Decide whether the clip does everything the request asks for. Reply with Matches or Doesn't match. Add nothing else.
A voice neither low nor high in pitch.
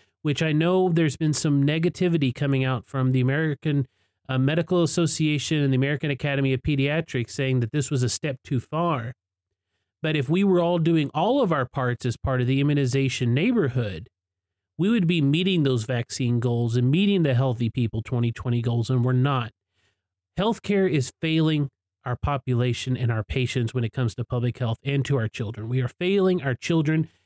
Doesn't match